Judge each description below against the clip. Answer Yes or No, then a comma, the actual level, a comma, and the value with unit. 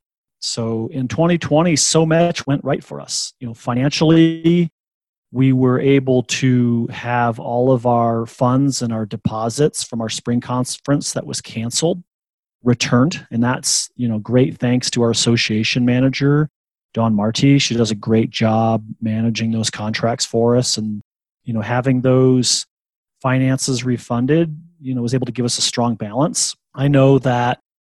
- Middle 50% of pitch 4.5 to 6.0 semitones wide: No, average, 2.9 semitones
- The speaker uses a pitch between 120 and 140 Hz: Yes, low, 125 Hz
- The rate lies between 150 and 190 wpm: Yes, average, 160 wpm